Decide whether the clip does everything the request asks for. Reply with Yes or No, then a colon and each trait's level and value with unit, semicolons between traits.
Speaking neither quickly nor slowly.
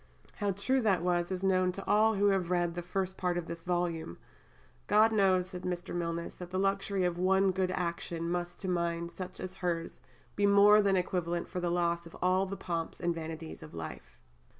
No: fast, 210 wpm